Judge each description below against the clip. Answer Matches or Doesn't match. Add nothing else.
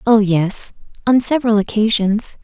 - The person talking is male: Doesn't match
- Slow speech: Matches